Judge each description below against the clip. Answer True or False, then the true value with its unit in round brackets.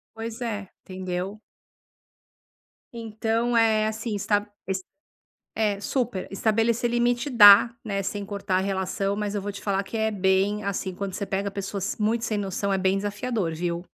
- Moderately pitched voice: False (205 Hz)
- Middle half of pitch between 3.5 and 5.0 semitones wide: False (2.4 semitones)